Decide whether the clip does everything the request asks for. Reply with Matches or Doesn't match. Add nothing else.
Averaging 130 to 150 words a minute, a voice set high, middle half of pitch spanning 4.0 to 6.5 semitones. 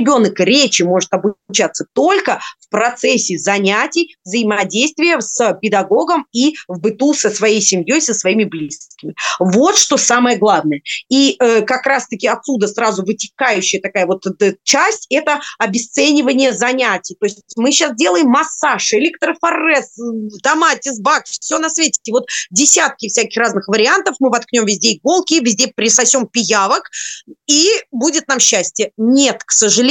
Matches